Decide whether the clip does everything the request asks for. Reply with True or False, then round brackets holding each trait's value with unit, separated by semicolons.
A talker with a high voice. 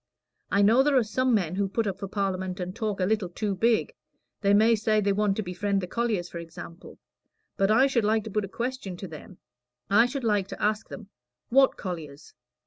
True (205 Hz)